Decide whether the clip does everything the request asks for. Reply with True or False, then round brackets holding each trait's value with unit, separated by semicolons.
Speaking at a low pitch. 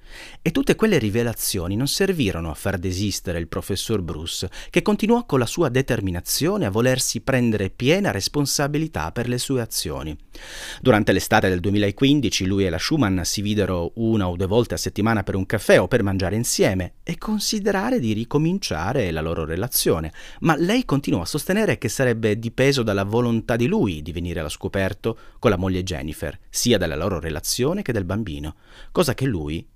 True (110 Hz)